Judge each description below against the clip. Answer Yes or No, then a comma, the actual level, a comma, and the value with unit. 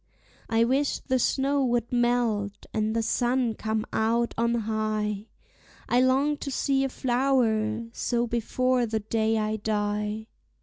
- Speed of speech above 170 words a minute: No, average, 140 wpm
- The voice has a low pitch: No, high, 230 Hz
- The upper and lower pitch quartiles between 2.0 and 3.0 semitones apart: Yes, narrow, 2.6 semitones